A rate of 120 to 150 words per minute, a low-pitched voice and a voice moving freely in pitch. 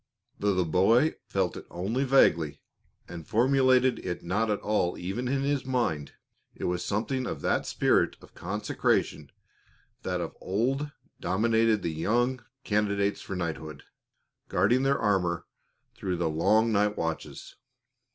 Yes: average, 140 wpm; low, 105 Hz; wide, 5.7 semitones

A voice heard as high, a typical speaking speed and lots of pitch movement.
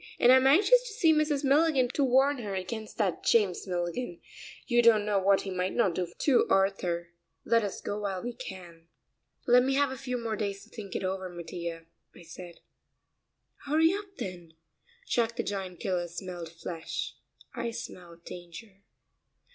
Yes: high, 200 Hz; average, 170 wpm; wide, 6.1 semitones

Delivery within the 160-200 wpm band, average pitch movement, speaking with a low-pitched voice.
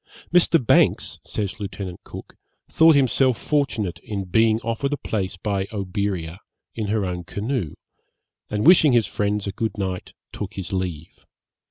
No: average, 150 wpm; average, 3.6 semitones; low, 105 Hz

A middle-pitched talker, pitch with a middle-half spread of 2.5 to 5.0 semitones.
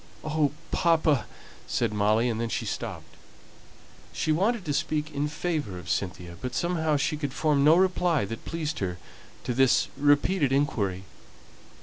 No: medium, 145 Hz; wide, 5.6 semitones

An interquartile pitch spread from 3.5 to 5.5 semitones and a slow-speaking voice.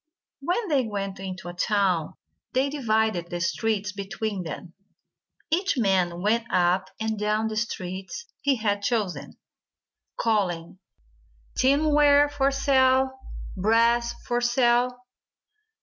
Yes: average, 5.2 semitones; slow, 115 wpm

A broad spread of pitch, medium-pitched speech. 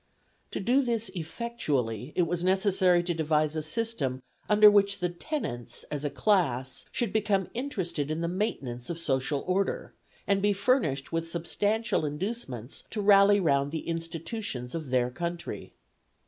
Yes: wide, 5.8 semitones; medium, 175 Hz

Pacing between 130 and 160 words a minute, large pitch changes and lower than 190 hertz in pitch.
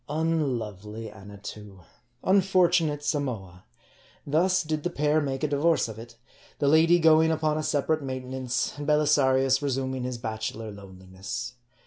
Yes: slow, 135 wpm; wide, 5.7 semitones; low, 135 Hz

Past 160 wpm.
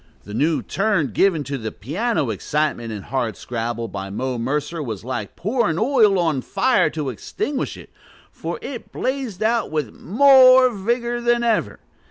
No: average, 155 wpm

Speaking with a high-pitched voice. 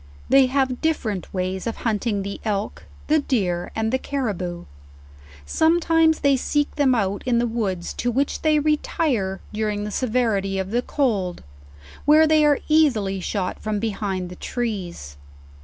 Yes: high, 225 Hz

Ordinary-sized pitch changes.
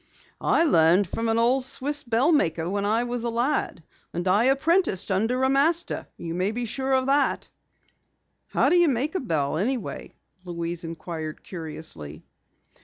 No: wide, 7.8 semitones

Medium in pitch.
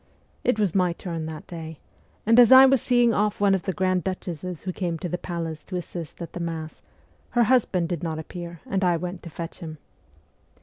Yes: medium, 180 Hz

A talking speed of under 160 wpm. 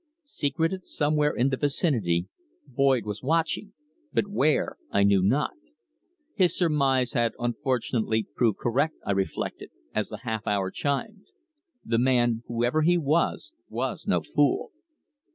Yes: slow, 135 wpm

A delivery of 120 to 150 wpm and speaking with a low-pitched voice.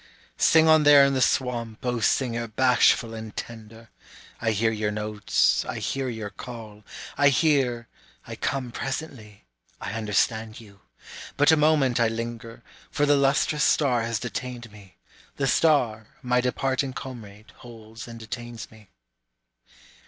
Yes: average, 145 wpm; low, 120 Hz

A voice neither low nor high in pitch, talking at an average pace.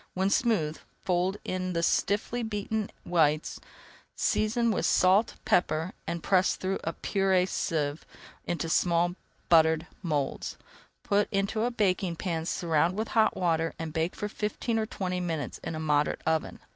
Yes: medium, 180 Hz; average, 155 wpm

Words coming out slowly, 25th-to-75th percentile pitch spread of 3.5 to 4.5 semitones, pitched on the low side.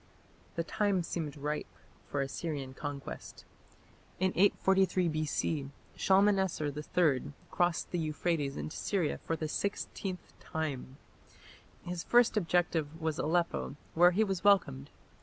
No: slow, 120 wpm; average, 3.9 semitones; medium, 165 Hz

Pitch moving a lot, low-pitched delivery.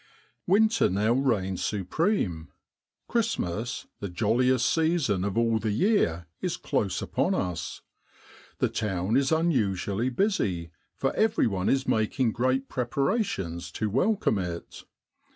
Yes: wide, 6.6 semitones; low, 115 Hz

